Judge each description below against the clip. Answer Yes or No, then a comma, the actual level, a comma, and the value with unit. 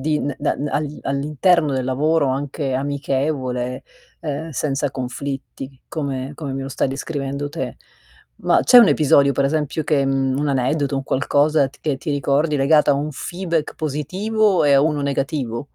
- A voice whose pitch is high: No, medium, 140 Hz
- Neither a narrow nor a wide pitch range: No, narrow, 2.1 semitones